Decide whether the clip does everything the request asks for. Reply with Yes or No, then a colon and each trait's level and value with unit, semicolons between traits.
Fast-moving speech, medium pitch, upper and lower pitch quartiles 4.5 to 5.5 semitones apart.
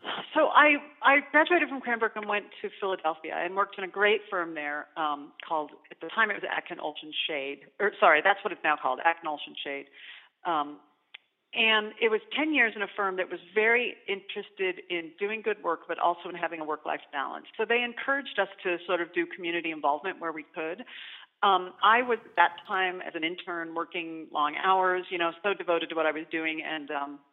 Yes: fast, 215 wpm; medium, 180 Hz; average, 4.8 semitones